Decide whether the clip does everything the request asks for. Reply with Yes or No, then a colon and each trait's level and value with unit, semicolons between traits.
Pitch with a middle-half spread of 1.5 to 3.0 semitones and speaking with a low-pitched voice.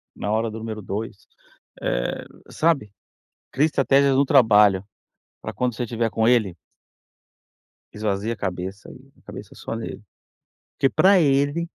No: average, 4.7 semitones; low, 115 Hz